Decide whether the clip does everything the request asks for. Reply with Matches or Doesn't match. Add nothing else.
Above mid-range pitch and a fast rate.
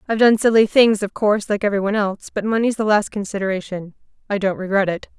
Matches